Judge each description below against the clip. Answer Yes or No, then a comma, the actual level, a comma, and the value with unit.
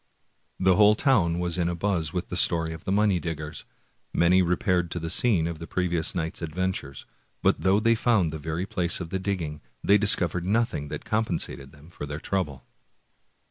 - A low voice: Yes, very low, 85 Hz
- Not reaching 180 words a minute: No, average, 190 wpm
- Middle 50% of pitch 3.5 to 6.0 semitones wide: No, average, 3.0 semitones